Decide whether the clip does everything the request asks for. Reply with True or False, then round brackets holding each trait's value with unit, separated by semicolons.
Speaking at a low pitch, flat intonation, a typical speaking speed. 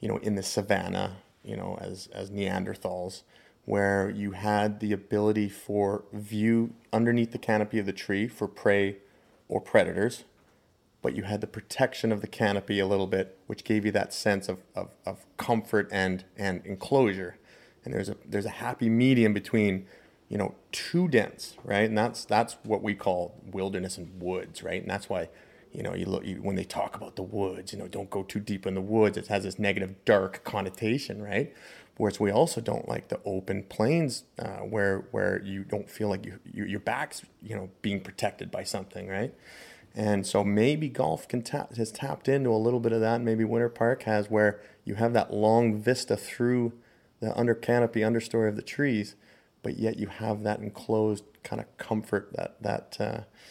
True (105 Hz; 2.3 semitones; 195 wpm)